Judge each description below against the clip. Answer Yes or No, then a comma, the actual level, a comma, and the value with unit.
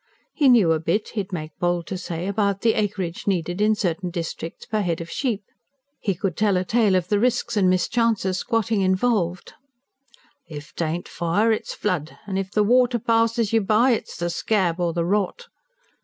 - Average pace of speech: Yes, average, 185 wpm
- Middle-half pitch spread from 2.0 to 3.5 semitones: No, average, 4.0 semitones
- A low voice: No, high, 195 Hz